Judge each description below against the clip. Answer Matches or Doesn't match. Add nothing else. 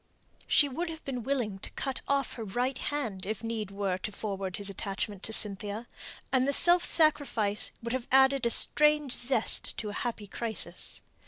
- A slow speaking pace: Doesn't match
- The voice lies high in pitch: Matches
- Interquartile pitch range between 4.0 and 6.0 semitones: Matches